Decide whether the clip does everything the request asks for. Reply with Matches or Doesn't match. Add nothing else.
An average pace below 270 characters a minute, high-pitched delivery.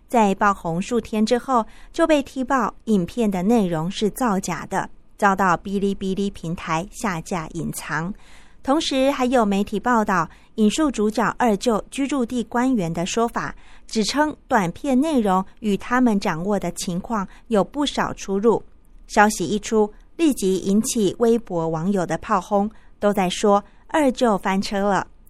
Matches